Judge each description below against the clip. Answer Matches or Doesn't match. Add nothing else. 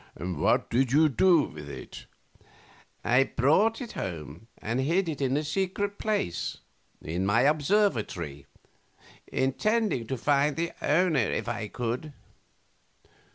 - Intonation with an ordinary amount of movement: Doesn't match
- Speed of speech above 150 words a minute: Doesn't match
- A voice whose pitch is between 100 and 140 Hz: Matches